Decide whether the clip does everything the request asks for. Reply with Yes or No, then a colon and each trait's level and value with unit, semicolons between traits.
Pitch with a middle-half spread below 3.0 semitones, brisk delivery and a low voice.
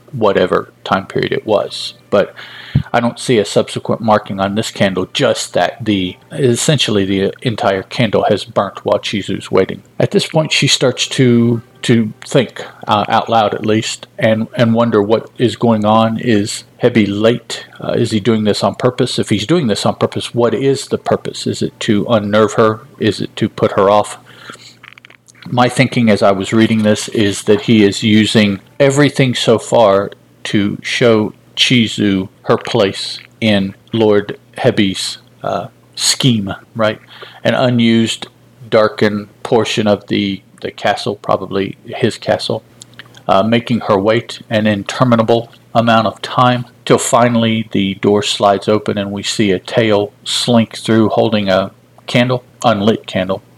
No: narrow, 2.5 semitones; average, 160 wpm; low, 110 Hz